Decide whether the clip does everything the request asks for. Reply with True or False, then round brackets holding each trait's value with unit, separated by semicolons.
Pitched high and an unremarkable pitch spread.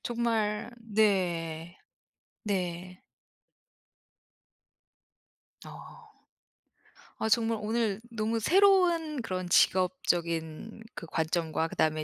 True (205 Hz; 5.0 semitones)